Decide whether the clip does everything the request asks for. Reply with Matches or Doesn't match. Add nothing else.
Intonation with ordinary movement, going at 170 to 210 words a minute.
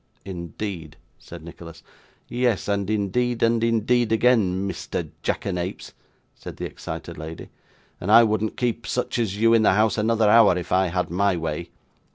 Doesn't match